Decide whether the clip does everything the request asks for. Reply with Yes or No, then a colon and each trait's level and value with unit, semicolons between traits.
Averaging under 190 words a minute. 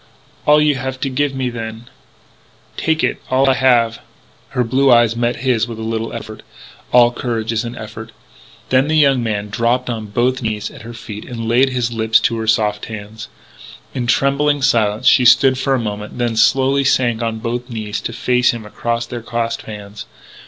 No: average, 195 wpm